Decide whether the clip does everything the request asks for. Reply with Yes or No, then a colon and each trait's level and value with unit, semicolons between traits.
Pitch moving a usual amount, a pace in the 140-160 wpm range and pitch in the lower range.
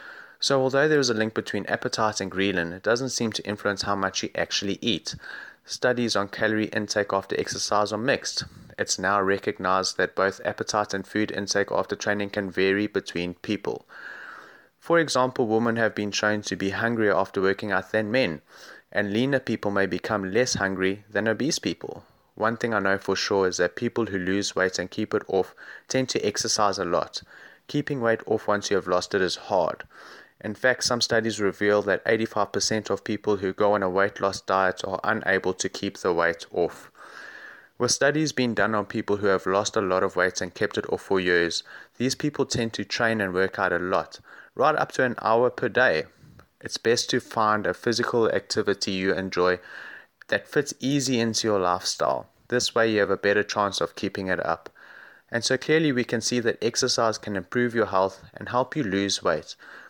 No: average, 3.2 semitones; average, 200 wpm; low, 105 Hz